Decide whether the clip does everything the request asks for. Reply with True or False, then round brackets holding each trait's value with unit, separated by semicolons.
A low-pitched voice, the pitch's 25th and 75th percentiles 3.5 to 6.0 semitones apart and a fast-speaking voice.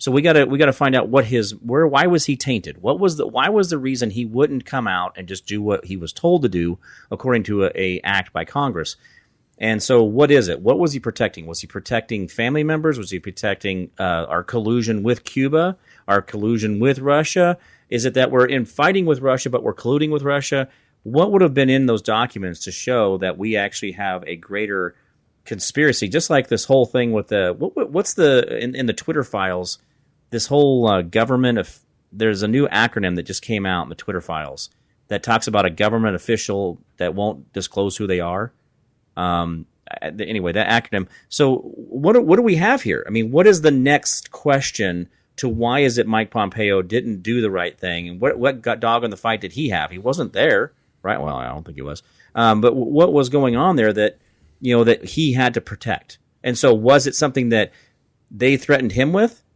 True (115 Hz; 5.3 semitones; 220 wpm)